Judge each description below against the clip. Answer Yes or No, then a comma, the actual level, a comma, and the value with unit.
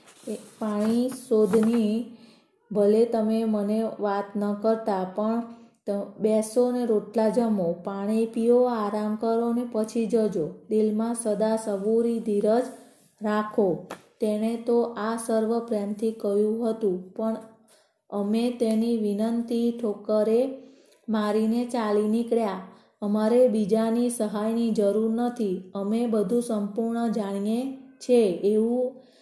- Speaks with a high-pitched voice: Yes, high, 225 Hz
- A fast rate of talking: No, average, 105 wpm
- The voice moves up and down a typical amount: No, narrow, 1.7 semitones